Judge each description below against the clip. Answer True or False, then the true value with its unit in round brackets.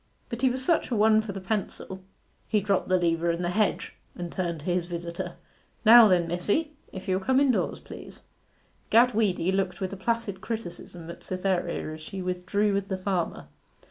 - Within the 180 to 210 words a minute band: True (190 wpm)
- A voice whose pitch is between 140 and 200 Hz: True (190 Hz)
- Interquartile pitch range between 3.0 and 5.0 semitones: True (3.6 semitones)